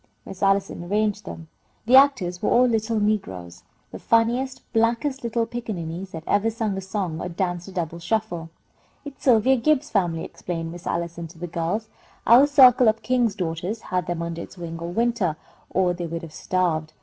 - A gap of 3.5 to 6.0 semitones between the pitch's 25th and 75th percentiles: Yes, average, 5.2 semitones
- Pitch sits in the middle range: No, high, 195 Hz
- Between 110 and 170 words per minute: No, average, 185 wpm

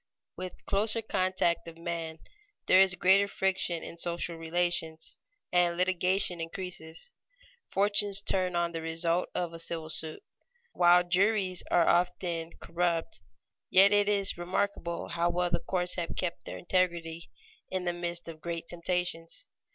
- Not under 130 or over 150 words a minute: Yes, average, 145 wpm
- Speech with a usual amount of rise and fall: No, narrow, 1.8 semitones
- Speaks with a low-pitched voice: No, medium, 175 Hz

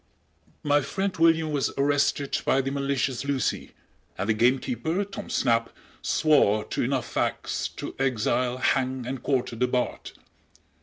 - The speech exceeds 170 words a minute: No, average, 140 wpm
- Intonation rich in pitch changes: No, narrow, 2.6 semitones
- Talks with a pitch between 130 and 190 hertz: Yes, low, 135 Hz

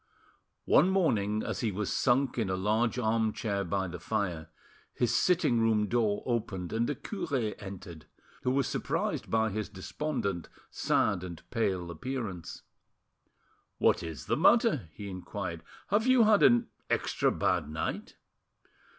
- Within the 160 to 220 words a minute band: No, average, 140 wpm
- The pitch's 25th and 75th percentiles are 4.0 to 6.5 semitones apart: Yes, average, 4.5 semitones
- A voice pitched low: Yes, low, 110 Hz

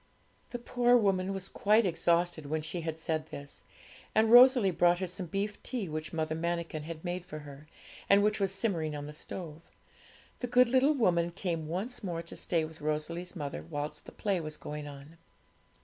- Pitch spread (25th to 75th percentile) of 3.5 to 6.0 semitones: Yes, average, 4.3 semitones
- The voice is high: No, medium, 170 Hz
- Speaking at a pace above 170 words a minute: Yes, average, 190 wpm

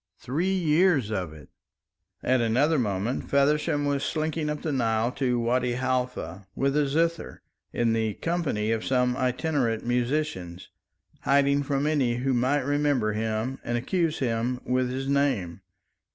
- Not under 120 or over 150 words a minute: Yes, average, 145 wpm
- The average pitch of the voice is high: No, low, 130 Hz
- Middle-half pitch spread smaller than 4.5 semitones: Yes, average, 3.9 semitones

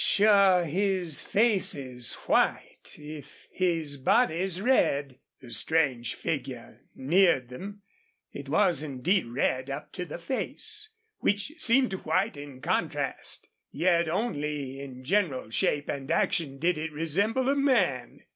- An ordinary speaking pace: No, slow, 125 wpm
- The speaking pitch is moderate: Yes, medium, 160 Hz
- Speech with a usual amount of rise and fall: No, wide, 6.3 semitones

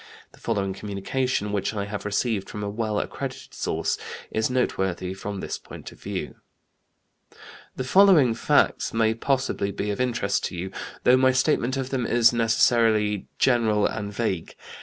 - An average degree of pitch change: Yes, average, 3.6 semitones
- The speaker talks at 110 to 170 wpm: Yes, average, 160 wpm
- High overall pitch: No, low, 110 Hz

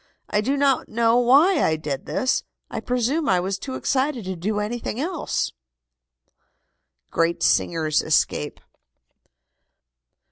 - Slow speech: Yes, slow, 120 wpm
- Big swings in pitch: Yes, wide, 7.2 semitones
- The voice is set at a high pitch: Yes, high, 230 Hz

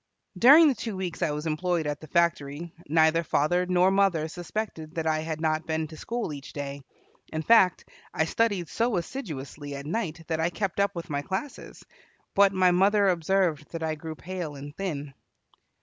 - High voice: No, medium, 165 Hz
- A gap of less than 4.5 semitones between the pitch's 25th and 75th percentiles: Yes, average, 3.5 semitones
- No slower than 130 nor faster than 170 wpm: No, average, 185 wpm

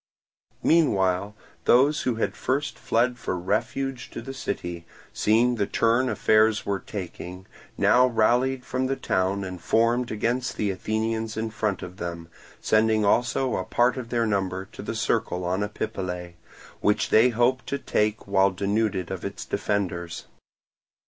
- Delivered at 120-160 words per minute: Yes, average, 155 wpm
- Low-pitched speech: Yes, low, 110 Hz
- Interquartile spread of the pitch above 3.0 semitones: Yes, average, 4.2 semitones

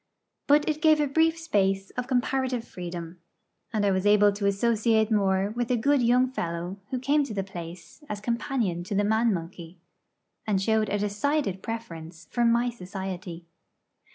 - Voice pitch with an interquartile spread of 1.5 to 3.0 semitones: No, average, 4.6 semitones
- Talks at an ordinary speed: Yes, average, 170 wpm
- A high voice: Yes, high, 210 Hz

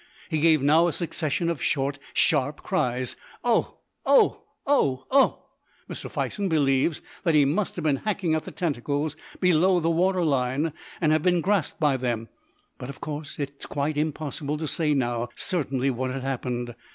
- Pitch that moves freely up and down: No, average, 3.7 semitones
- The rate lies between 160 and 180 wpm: Yes, average, 175 wpm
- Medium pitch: Yes, medium, 150 Hz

